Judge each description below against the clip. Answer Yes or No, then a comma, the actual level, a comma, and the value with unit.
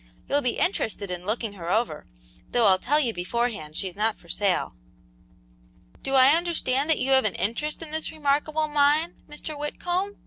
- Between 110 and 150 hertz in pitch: No, very high, 265 Hz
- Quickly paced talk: No, average, 175 wpm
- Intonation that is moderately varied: No, wide, 6.6 semitones